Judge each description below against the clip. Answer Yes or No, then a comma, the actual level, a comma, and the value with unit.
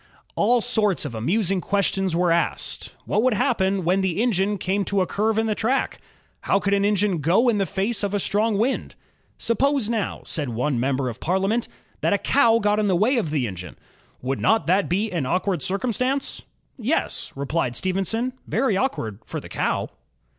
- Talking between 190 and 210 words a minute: Yes, average, 195 wpm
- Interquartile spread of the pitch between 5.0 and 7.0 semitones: No, average, 4.3 semitones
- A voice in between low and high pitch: No, high, 200 Hz